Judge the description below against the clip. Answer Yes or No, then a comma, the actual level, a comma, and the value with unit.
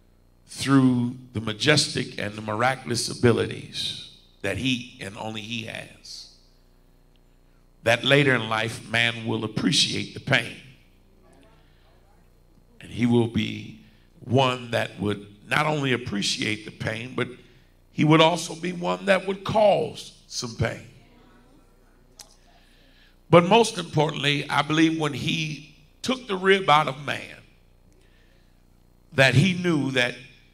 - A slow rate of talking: Yes, slow, 120 wpm